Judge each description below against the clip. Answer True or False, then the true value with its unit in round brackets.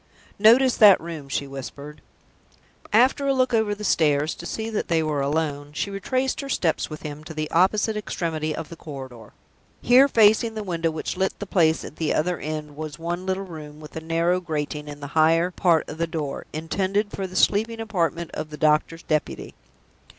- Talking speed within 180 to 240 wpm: True (195 wpm)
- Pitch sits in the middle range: True (165 Hz)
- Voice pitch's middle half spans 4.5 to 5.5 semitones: True (5.0 semitones)